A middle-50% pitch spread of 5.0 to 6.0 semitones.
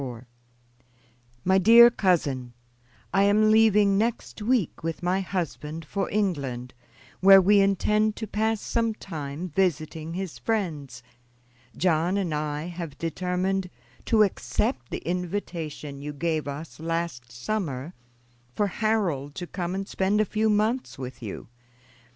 Yes: average, 5.3 semitones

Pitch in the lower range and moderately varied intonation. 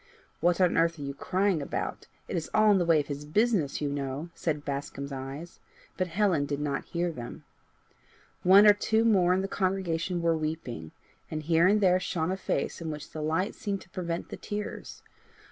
No: medium, 170 Hz; average, 4.3 semitones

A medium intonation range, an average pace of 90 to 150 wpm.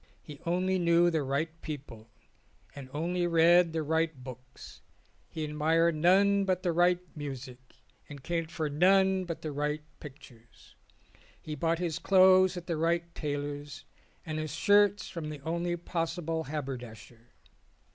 Yes: average, 3.1 semitones; average, 145 wpm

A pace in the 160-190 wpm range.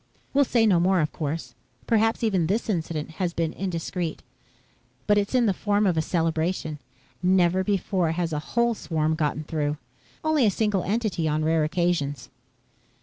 Yes: average, 165 wpm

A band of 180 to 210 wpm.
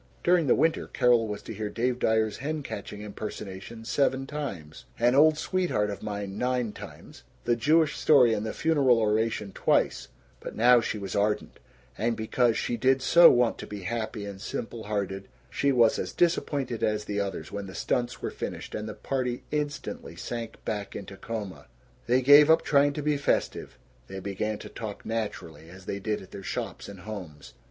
Yes: average, 185 wpm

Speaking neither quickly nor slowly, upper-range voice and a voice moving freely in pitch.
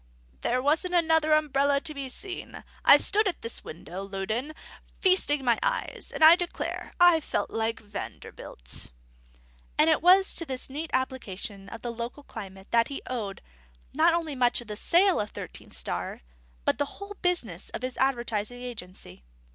Yes: average, 165 wpm; very high, 265 Hz; wide, 6.5 semitones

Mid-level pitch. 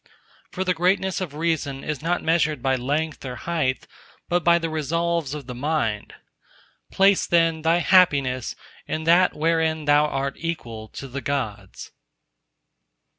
Yes: medium, 155 Hz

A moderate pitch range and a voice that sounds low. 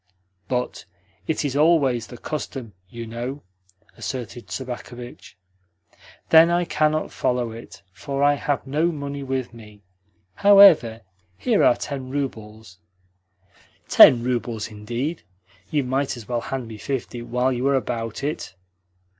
Yes: average, 3.4 semitones; low, 125 Hz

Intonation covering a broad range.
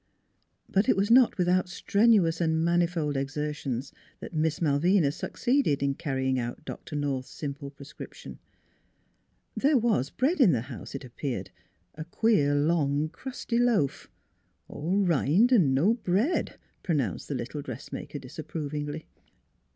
Yes: wide, 5.8 semitones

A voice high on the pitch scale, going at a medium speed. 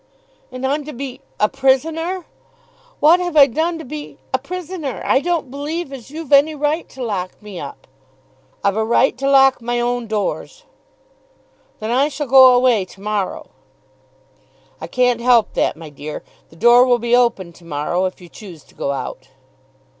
Yes: very high, 250 Hz; average, 175 wpm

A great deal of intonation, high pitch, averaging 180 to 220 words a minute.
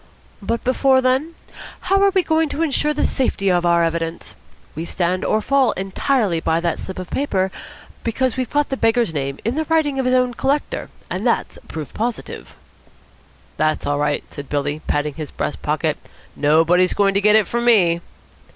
Yes: wide, 7.9 semitones; high, 210 Hz; average, 185 wpm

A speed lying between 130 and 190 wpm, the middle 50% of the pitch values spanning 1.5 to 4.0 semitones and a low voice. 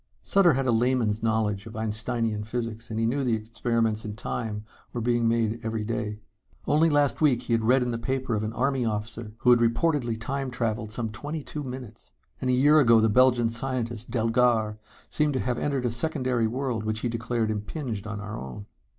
No: average, 200 wpm; narrow, 2.6 semitones; low, 115 Hz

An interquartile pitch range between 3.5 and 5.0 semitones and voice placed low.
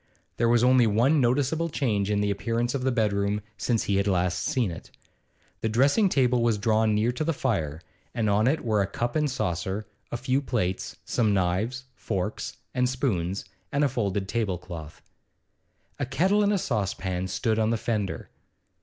Yes: average, 4.3 semitones; low, 115 Hz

